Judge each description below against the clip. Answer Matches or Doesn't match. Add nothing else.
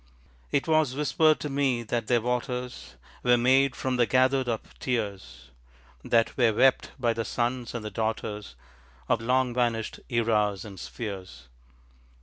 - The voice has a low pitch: Matches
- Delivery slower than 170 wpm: Matches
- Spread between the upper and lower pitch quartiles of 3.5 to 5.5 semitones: Doesn't match